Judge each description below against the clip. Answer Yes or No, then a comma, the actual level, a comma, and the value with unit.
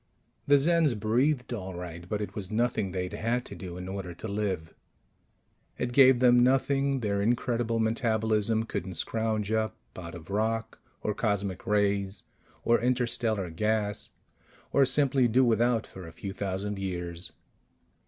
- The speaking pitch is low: Yes, low, 110 Hz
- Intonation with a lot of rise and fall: No, average, 3.9 semitones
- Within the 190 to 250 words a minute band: No, average, 150 wpm